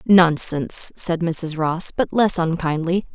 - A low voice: No, medium, 170 Hz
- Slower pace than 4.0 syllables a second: Yes, 3.8 syllables/s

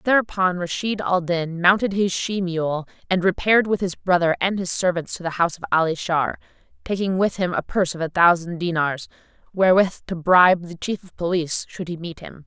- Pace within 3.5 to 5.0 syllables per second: No, 5.5 syllables/s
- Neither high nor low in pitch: Yes, medium, 180 Hz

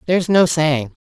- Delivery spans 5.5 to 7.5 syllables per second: No, 5.1 syllables/s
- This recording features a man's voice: No, female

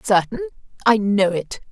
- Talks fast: No, slow, 105 wpm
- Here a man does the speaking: No, female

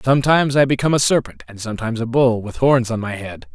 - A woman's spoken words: No, male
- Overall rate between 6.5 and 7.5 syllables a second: Yes, 6.8 syllables/s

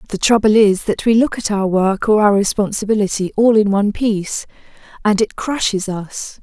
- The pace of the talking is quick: No, average, 185 wpm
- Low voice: No, high, 210 Hz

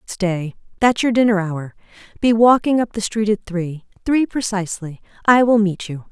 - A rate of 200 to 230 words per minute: No, average, 175 wpm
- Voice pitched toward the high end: Yes, high, 205 Hz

